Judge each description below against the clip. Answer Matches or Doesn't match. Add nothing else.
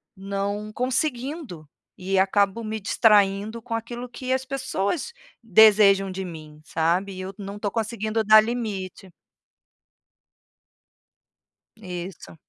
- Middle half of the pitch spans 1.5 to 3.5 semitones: Matches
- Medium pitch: Doesn't match